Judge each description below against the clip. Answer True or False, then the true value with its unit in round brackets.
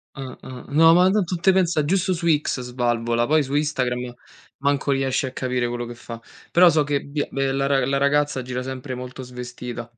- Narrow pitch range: False (3.3 semitones)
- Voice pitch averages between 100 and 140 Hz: True (135 Hz)